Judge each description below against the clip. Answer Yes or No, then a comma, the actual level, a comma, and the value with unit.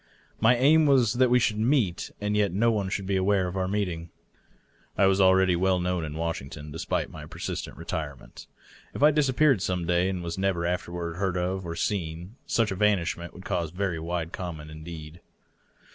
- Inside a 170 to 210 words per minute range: Yes, average, 190 wpm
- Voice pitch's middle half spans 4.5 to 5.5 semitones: No, average, 3.5 semitones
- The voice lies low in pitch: Yes, very low, 95 Hz